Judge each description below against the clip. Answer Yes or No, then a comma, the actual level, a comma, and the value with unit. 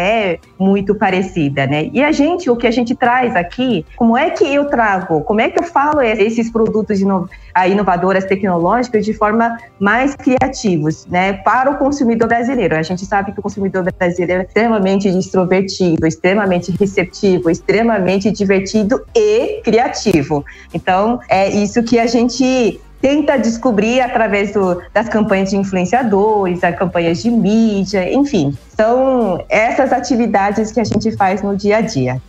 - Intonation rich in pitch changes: No, average, 4.3 semitones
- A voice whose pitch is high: Yes, high, 205 Hz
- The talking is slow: No, average, 155 wpm